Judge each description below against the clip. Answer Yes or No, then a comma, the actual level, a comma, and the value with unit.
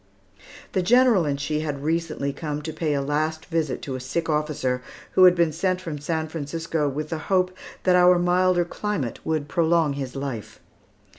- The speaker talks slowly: No, average, 180 wpm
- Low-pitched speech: No, medium, 160 Hz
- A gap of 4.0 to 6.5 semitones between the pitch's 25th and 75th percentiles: No, average, 3.3 semitones